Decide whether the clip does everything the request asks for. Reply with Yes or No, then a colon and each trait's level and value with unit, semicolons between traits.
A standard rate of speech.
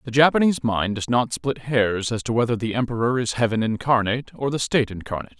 No: fast, 210 wpm